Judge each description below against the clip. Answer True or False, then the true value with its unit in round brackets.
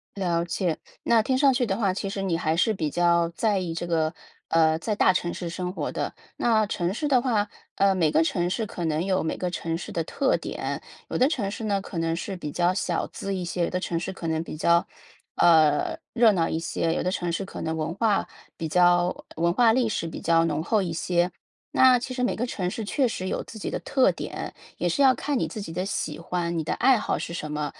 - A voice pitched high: False (180 Hz)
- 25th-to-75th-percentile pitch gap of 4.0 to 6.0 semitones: True (4.4 semitones)